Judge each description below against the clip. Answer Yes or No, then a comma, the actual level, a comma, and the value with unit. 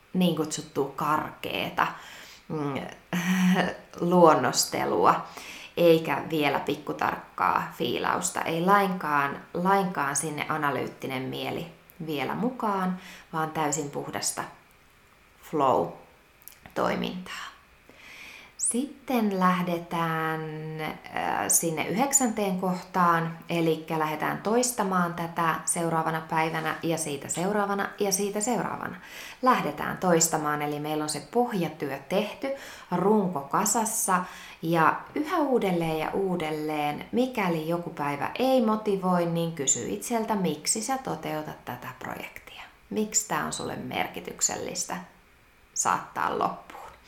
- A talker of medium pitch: Yes, medium, 170 Hz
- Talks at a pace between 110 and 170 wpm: No, slow, 95 wpm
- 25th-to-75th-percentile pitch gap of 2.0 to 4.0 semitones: No, average, 4.5 semitones